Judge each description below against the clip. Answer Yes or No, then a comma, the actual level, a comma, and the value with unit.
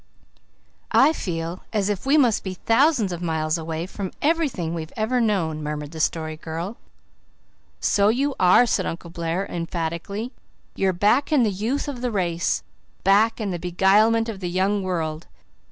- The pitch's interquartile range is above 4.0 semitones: Yes, average, 5.2 semitones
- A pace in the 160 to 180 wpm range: Yes, average, 165 wpm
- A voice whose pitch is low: No, high, 190 Hz